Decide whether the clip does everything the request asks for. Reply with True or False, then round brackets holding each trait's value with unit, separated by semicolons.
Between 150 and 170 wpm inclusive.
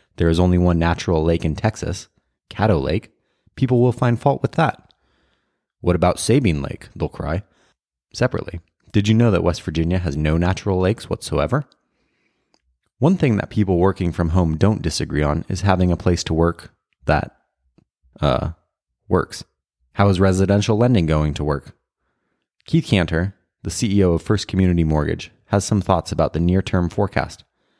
True (160 wpm)